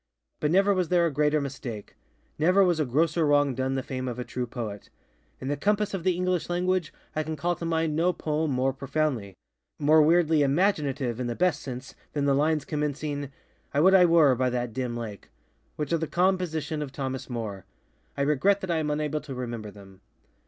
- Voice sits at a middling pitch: Yes, medium, 150 Hz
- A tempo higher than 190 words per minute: Yes, average, 200 wpm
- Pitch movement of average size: Yes, average, 4.3 semitones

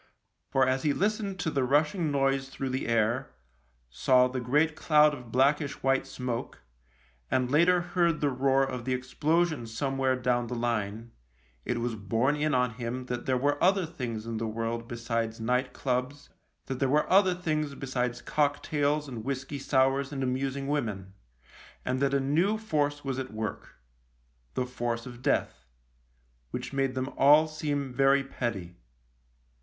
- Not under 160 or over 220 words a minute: Yes, average, 165 wpm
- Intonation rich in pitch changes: No, average, 3.3 semitones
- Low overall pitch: Yes, low, 130 Hz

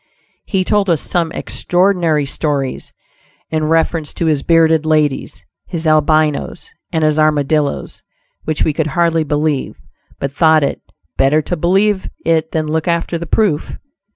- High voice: No, medium, 160 Hz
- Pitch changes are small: Yes, narrow, 1.9 semitones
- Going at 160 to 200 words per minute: No, average, 145 wpm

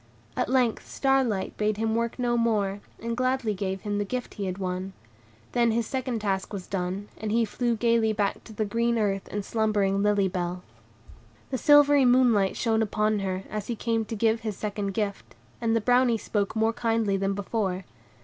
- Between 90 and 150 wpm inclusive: No, average, 195 wpm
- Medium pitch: No, high, 215 Hz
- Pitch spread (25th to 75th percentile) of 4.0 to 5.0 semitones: No, average, 2.8 semitones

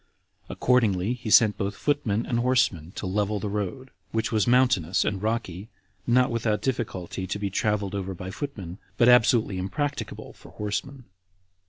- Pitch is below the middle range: Yes, low, 105 Hz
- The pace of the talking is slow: No, average, 160 wpm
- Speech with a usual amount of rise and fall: Yes, average, 4.1 semitones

